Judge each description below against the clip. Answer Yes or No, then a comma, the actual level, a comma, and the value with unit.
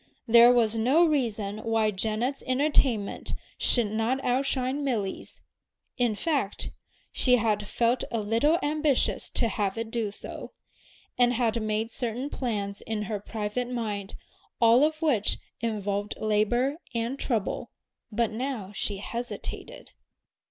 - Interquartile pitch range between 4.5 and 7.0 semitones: No, average, 3.3 semitones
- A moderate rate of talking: No, slow, 130 wpm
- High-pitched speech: Yes, high, 230 Hz